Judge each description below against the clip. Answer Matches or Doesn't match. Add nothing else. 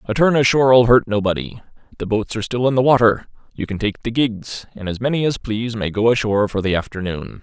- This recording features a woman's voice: Doesn't match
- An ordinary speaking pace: Doesn't match